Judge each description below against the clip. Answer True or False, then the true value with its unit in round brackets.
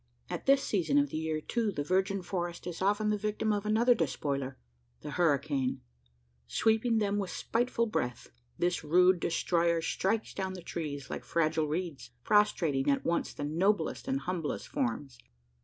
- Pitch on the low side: False (180 Hz)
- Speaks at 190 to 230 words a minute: False (160 wpm)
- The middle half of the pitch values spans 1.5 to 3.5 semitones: False (5.4 semitones)